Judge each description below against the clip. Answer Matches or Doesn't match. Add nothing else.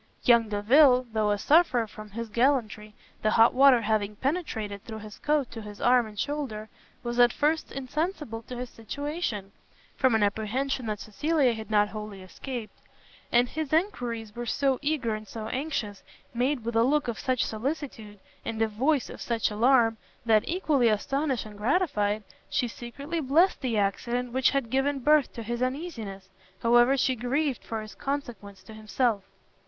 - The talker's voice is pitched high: Matches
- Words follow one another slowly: Doesn't match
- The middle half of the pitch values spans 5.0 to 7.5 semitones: Doesn't match